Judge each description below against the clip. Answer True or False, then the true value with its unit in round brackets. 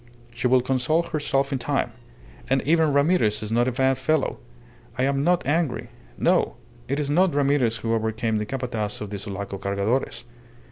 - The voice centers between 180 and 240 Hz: False (130 Hz)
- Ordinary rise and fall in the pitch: True (4.2 semitones)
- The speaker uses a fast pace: False (175 wpm)